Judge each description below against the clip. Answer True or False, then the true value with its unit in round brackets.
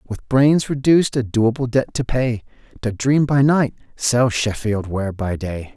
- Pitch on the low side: True (120 Hz)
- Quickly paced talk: False (175 wpm)